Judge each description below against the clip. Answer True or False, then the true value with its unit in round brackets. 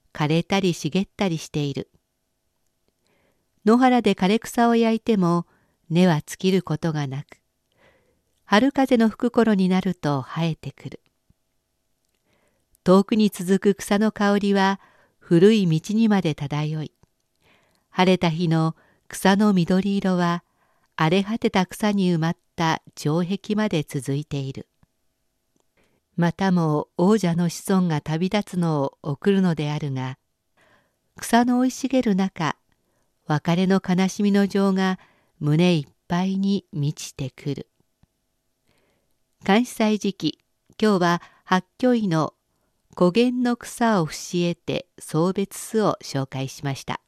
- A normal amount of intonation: True (4.5 semitones)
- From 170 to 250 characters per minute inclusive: True (225 characters per minute)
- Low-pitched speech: False (185 Hz)